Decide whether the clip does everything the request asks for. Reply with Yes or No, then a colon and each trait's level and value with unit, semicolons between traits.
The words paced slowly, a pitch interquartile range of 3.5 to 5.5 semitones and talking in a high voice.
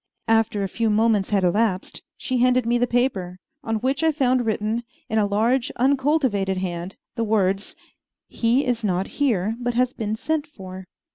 No: average, 170 wpm; average, 4.1 semitones; high, 225 Hz